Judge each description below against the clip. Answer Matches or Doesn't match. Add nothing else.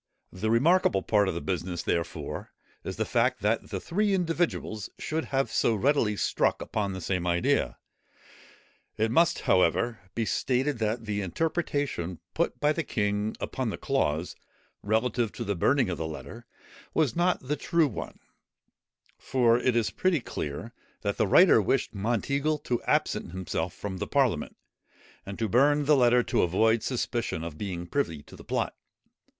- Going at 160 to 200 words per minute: Matches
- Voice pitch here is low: Matches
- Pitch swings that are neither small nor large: Doesn't match